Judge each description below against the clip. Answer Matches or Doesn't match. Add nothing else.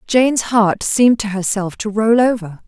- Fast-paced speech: Doesn't match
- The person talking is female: Matches